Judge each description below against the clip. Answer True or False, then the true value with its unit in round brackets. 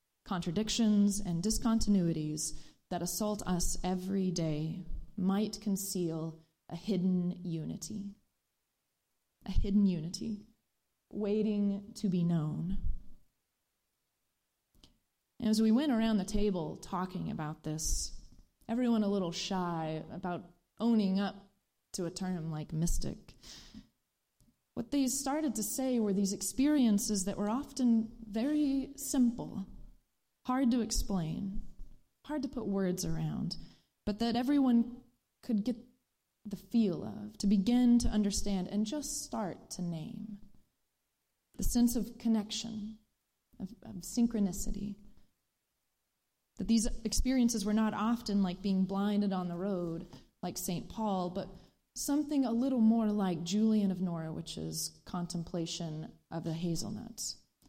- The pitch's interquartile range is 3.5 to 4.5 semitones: True (3.9 semitones)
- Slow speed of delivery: True (120 wpm)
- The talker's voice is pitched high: True (205 Hz)